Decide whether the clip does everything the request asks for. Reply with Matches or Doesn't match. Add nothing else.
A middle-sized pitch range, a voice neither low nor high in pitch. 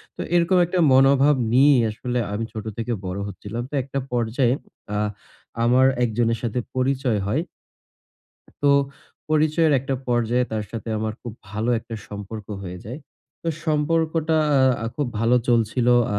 Doesn't match